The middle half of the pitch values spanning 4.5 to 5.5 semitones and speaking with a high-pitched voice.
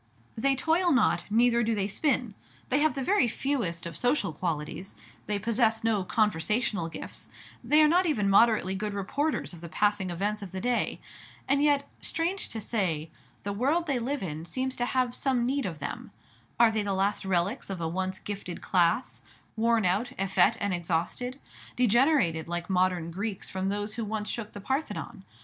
Yes: average, 5.2 semitones; high, 210 Hz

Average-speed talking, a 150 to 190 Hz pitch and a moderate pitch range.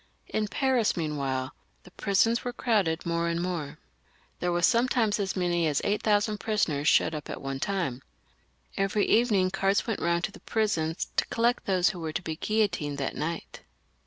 Yes: average, 180 wpm; medium, 185 Hz; average, 4.8 semitones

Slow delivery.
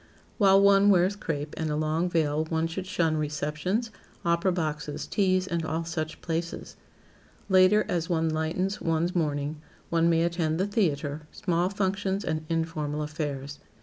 No: average, 150 wpm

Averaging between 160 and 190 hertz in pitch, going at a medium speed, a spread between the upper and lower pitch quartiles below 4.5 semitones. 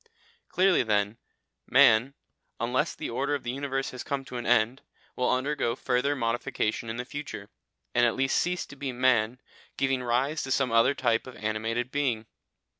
No: low, 125 Hz; average, 175 wpm; average, 2.9 semitones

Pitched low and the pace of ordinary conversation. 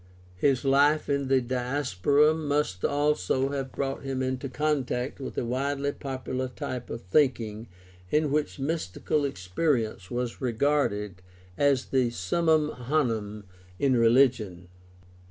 No: low, 130 Hz; slow, 125 wpm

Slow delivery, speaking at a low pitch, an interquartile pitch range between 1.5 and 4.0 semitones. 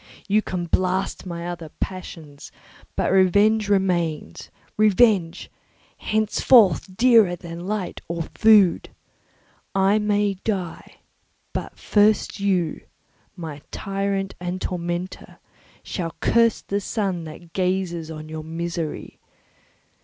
No: slow, 100 wpm; medium, 185 Hz; average, 3.2 semitones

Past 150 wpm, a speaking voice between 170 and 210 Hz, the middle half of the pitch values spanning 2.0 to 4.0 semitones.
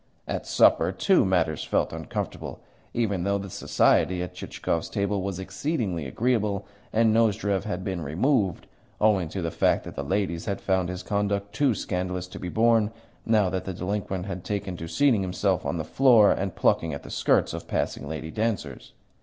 No: average, 180 wpm; very low, 95 Hz; average, 2.8 semitones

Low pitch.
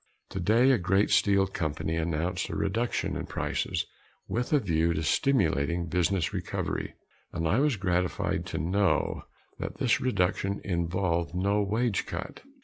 Yes: very low, 95 Hz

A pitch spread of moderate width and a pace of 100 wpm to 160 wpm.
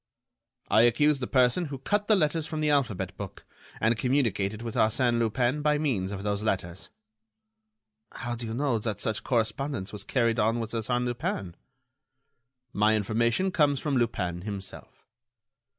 Yes: average, 4.6 semitones; average, 155 wpm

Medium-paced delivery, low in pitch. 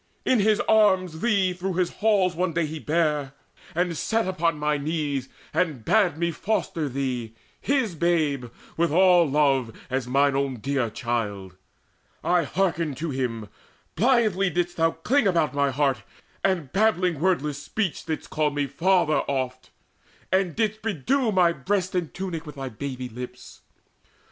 No: average, 155 wpm; medium, 165 Hz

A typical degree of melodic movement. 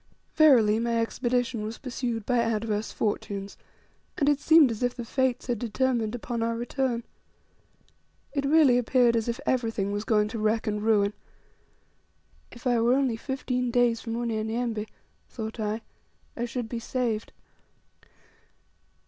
No: narrow, 2.2 semitones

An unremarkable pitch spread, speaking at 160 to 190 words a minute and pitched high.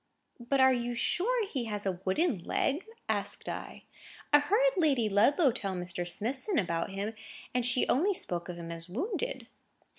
No: wide, 8.9 semitones; average, 170 wpm; high, 240 Hz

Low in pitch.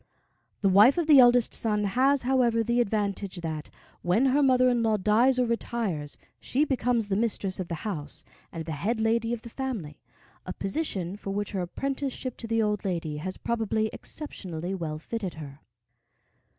No: high, 220 Hz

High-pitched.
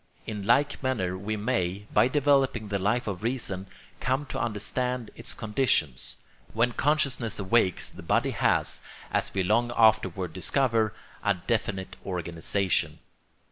No: low, 110 Hz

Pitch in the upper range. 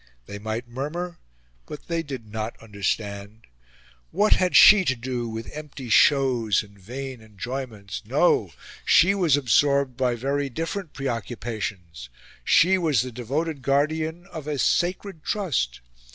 No: low, 130 Hz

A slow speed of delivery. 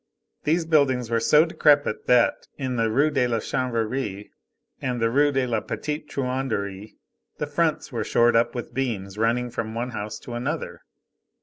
No: average, 170 wpm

